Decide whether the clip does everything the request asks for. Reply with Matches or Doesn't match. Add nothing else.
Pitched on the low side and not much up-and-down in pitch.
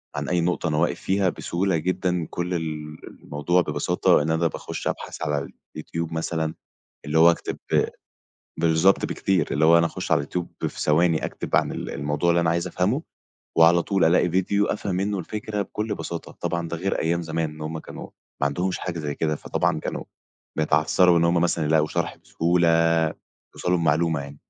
Matches